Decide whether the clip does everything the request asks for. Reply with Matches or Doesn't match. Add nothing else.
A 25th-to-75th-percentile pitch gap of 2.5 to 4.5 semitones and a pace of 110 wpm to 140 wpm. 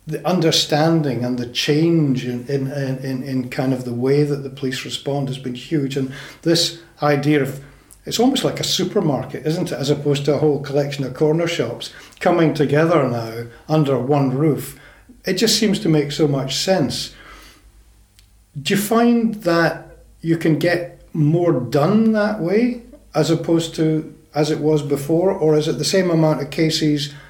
Doesn't match